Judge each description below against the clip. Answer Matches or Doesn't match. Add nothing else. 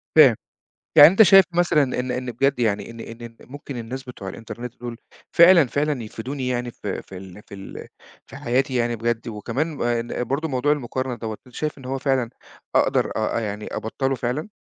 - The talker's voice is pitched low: Matches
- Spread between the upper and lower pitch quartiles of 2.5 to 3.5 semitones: Matches